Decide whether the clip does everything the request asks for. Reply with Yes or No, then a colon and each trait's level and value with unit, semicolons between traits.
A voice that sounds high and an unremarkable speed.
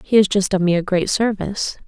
No: high, 195 Hz; fast, 255 wpm